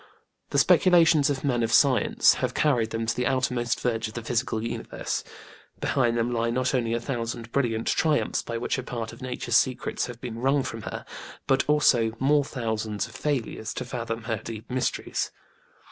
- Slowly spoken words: No, average, 185 wpm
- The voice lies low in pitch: Yes, low, 120 Hz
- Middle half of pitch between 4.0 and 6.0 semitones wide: No, narrow, 2.5 semitones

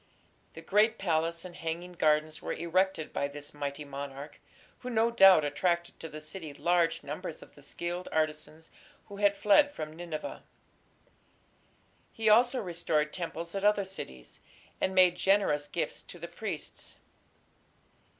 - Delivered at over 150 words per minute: No, average, 145 wpm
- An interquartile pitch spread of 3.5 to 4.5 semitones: Yes, average, 3.9 semitones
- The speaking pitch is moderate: Yes, medium, 170 Hz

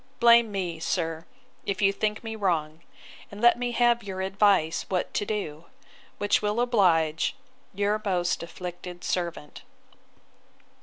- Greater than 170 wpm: No, slow, 135 wpm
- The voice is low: No, high, 195 Hz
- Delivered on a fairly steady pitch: No, average, 3.8 semitones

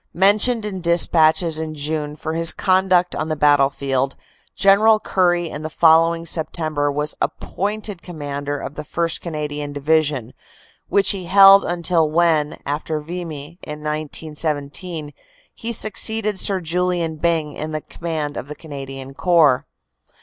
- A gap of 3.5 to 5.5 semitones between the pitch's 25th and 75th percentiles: No, average, 3.1 semitones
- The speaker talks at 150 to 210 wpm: No, slow, 135 wpm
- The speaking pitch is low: No, medium, 160 Hz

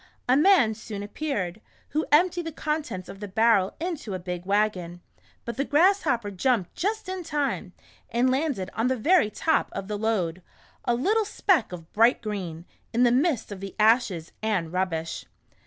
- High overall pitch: Yes, high, 225 Hz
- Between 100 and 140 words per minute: No, average, 175 wpm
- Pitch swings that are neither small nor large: No, wide, 7.7 semitones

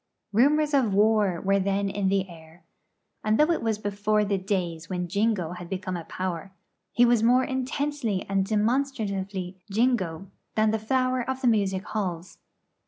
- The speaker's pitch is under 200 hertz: No, high, 205 Hz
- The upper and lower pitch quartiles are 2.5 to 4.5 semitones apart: Yes, average, 3.9 semitones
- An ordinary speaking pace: Yes, average, 165 wpm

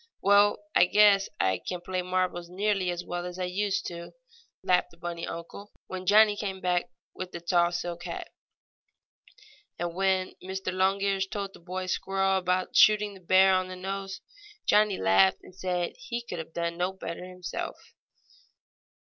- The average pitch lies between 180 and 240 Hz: Yes, medium, 185 Hz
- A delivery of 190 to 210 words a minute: No, average, 165 wpm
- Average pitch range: No, narrow, 1.7 semitones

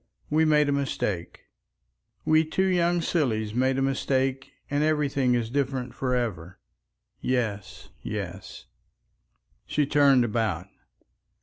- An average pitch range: Yes, average, 3.8 semitones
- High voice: No, low, 135 Hz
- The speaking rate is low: Yes, slow, 115 wpm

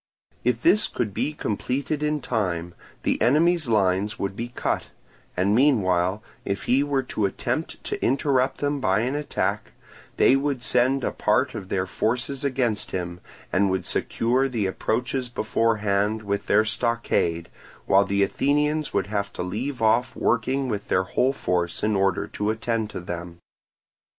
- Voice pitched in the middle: No, low, 110 Hz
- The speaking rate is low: No, average, 160 wpm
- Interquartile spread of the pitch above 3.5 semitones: Yes, average, 5.0 semitones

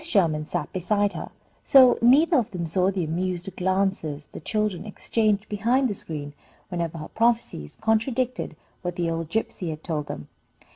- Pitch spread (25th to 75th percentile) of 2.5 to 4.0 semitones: No, average, 5.1 semitones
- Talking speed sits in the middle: Yes, average, 160 wpm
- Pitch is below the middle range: No, high, 190 Hz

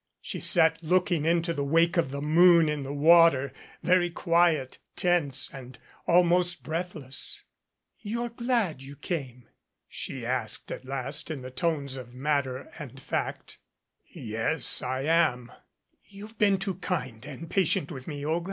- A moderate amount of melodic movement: Yes, average, 4.5 semitones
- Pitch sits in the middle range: Yes, medium, 160 Hz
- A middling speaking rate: Yes, average, 145 wpm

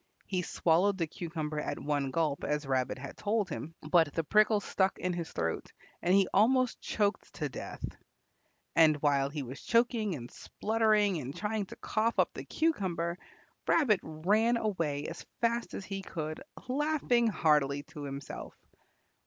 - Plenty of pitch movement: Yes, wide, 6.2 semitones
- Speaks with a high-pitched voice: No, medium, 175 Hz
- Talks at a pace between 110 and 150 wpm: No, average, 160 wpm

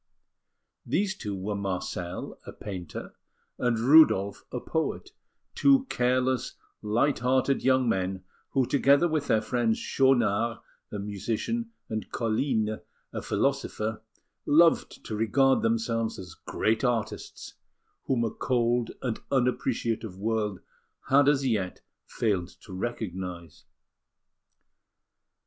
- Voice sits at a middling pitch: No, low, 115 Hz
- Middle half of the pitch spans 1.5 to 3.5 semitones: No, average, 4.1 semitones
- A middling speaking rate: No, slow, 110 wpm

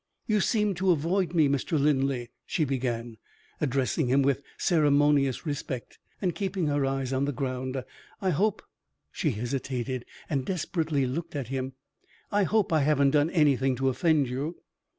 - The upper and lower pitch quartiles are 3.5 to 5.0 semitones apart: Yes, average, 3.9 semitones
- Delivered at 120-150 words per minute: No, average, 160 wpm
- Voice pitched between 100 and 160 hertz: Yes, medium, 140 Hz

